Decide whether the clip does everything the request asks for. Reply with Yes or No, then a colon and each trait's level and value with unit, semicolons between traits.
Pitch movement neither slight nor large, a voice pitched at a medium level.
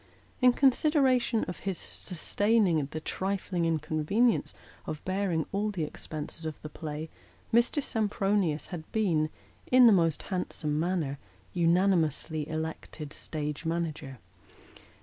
Yes: average, 4.6 semitones; medium, 170 Hz